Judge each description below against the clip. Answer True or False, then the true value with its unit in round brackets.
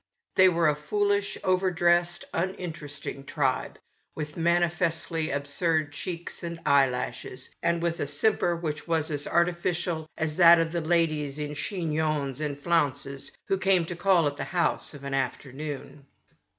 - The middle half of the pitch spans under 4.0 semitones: True (2.9 semitones)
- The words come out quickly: False (160 wpm)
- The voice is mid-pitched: True (160 Hz)